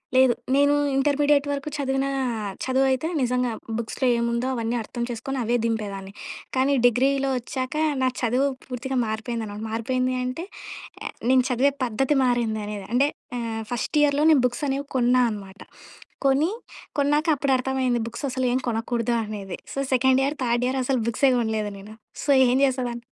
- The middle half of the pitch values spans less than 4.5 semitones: Yes, narrow, 2.6 semitones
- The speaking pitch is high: Yes, very high, 250 Hz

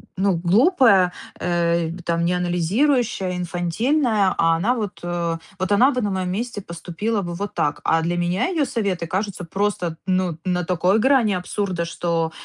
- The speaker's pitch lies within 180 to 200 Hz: Yes, medium, 185 Hz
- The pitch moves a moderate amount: Yes, average, 3.4 semitones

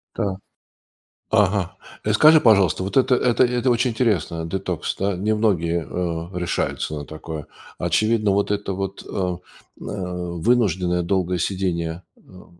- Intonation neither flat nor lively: Yes, average, 3.6 semitones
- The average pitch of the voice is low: Yes, very low, 95 Hz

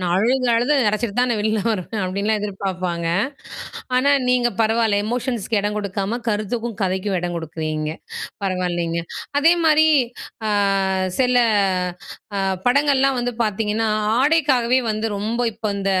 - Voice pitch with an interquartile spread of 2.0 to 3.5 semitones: No, average, 4.3 semitones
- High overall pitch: Yes, high, 215 Hz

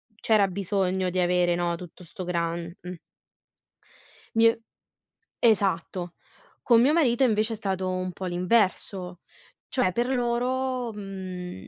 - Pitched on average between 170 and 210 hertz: Yes, high, 190 Hz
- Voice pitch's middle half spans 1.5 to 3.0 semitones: No, average, 4.2 semitones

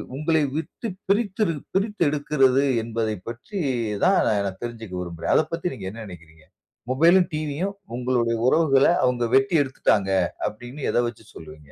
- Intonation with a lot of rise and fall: Yes, wide, 6.5 semitones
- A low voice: Yes, low, 130 Hz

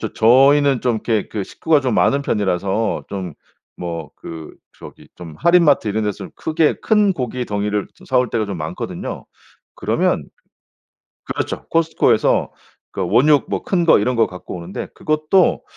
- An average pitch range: No, wide, 6.8 semitones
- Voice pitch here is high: No, low, 115 Hz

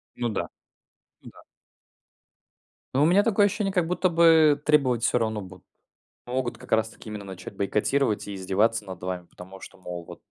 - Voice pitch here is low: Yes, low, 115 Hz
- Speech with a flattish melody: No, wide, 7.9 semitones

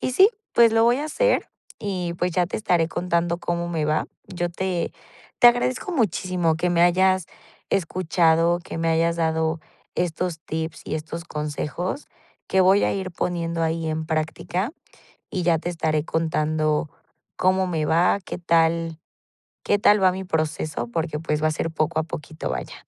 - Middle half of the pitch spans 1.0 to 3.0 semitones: Yes, narrow, 2.4 semitones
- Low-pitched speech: No, medium, 170 Hz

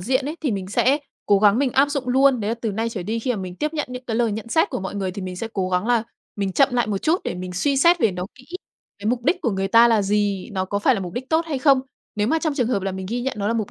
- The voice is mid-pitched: No, high, 225 Hz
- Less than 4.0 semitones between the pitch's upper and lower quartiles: No, average, 5.0 semitones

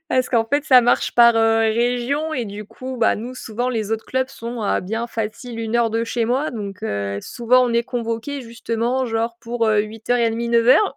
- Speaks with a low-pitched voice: No, high, 235 Hz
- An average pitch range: No, narrow, 1.7 semitones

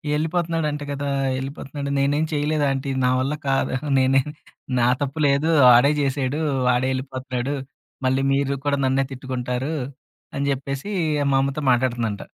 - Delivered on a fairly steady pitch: Yes, narrow, 1.8 semitones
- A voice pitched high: No, low, 135 Hz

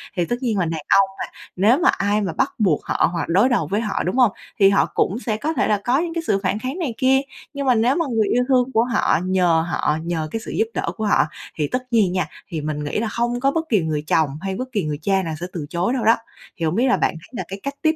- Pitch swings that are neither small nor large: No, wide, 6.2 semitones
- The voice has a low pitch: No, high, 210 Hz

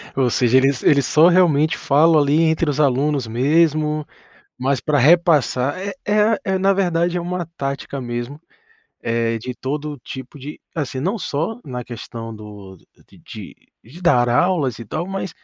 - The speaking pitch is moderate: Yes, medium, 145 Hz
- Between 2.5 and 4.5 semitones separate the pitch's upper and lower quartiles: No, average, 5.1 semitones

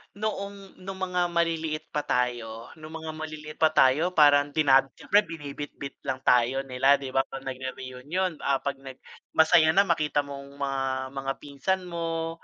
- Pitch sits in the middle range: Yes, medium, 150 Hz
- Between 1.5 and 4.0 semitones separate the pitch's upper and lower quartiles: Yes, average, 3.6 semitones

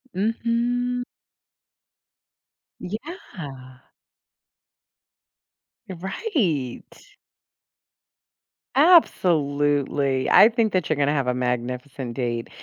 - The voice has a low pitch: No, medium, 150 Hz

